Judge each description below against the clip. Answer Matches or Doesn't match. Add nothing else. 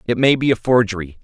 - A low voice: Matches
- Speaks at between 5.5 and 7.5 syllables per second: Matches